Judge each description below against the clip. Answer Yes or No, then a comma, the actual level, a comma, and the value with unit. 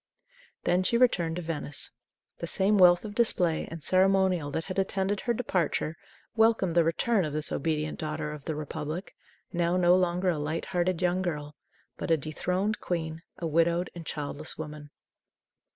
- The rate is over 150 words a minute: Yes, average, 170 wpm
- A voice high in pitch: No, medium, 175 Hz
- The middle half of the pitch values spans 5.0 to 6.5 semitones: No, average, 3.1 semitones